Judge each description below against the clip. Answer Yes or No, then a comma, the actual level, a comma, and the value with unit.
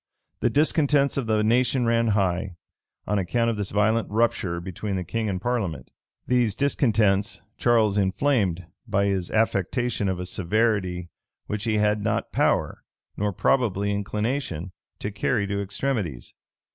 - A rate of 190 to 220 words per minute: No, average, 145 wpm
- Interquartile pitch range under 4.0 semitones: Yes, average, 3.5 semitones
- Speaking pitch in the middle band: No, low, 105 Hz